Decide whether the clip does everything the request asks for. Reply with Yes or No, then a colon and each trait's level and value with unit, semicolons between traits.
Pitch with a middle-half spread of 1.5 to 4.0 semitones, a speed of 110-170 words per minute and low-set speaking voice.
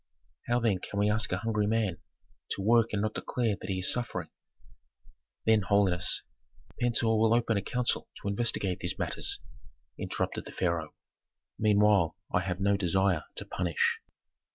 Yes: average, 3.1 semitones; average, 160 wpm; low, 105 Hz